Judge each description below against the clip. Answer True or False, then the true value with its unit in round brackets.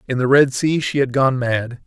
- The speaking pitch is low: True (130 Hz)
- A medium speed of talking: False (255 wpm)